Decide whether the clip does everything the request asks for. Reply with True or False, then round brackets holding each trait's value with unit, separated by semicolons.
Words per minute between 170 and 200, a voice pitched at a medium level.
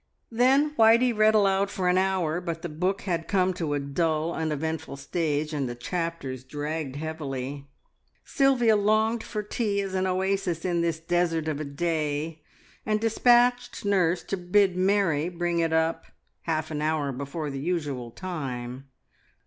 False (155 wpm; 170 Hz)